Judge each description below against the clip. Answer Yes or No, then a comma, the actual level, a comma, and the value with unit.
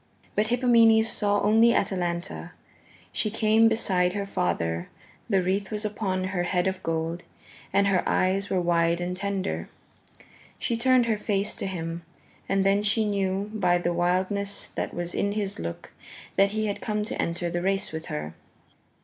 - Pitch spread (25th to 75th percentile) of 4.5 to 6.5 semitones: No, average, 3.1 semitones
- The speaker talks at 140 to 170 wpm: Yes, average, 165 wpm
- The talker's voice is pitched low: No, high, 195 Hz